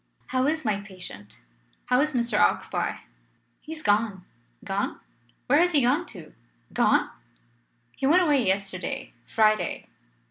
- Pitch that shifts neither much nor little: No, wide, 6.9 semitones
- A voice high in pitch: Yes, high, 235 Hz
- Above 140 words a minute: No, slow, 135 wpm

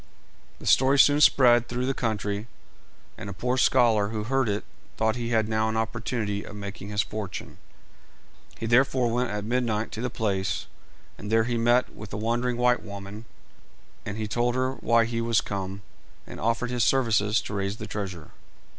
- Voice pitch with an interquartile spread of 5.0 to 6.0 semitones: No, average, 2.8 semitones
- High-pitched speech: No, low, 115 Hz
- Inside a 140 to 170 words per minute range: No, average, 180 wpm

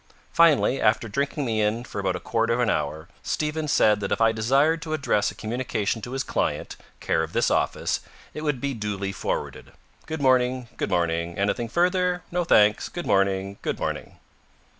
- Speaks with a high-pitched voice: No, low, 115 Hz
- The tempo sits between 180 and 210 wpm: Yes, average, 185 wpm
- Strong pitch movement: Yes, wide, 5.8 semitones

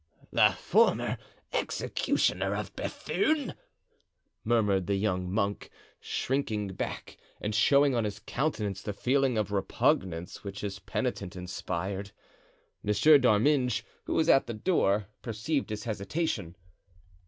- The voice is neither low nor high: No, low, 105 Hz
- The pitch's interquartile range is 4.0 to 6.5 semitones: Yes, average, 5.1 semitones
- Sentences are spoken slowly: Yes, slow, 120 wpm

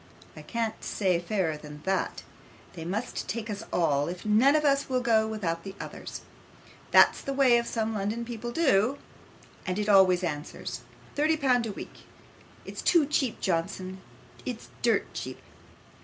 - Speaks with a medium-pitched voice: No, high, 215 Hz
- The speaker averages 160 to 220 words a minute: Yes, average, 165 wpm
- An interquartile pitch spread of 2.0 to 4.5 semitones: No, average, 5.0 semitones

